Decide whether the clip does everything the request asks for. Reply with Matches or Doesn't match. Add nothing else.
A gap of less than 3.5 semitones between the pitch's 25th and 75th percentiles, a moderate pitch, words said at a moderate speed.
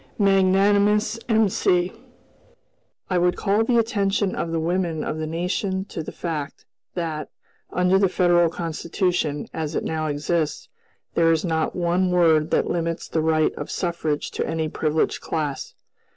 Matches